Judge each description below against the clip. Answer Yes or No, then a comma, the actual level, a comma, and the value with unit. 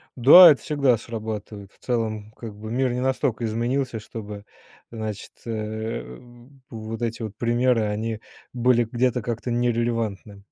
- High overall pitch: No, low, 115 Hz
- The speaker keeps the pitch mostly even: Yes, narrow, 2.1 semitones